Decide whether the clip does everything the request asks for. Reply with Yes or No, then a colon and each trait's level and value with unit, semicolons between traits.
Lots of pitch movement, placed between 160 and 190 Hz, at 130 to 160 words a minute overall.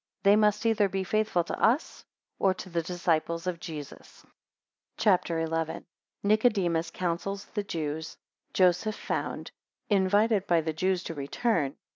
No: average, 3.8 semitones; medium, 185 Hz; average, 150 wpm